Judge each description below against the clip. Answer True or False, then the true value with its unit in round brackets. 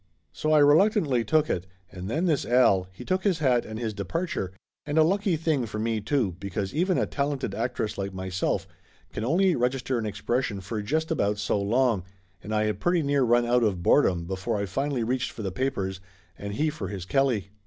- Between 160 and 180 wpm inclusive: False (205 wpm)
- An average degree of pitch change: False (6.4 semitones)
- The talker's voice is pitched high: False (120 Hz)